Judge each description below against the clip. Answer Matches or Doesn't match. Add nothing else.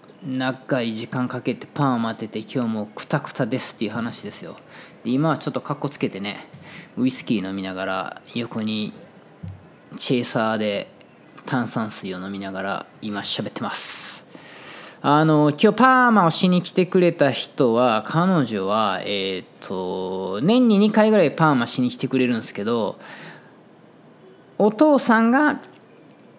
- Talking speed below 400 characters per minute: Matches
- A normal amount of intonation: Doesn't match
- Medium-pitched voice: Doesn't match